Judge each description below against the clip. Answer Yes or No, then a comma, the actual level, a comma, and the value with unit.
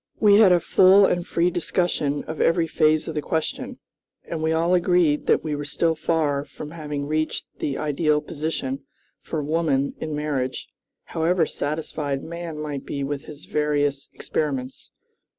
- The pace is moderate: Yes, average, 160 wpm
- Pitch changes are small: Yes, narrow, 2.3 semitones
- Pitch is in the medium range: Yes, medium, 155 Hz